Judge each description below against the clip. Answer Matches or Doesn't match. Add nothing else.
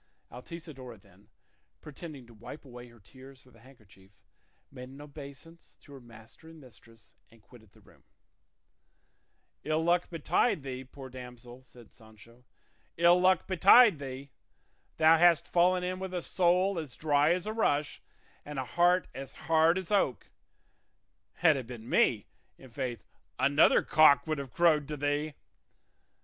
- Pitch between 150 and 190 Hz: Doesn't match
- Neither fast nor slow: Matches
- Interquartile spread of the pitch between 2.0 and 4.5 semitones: Doesn't match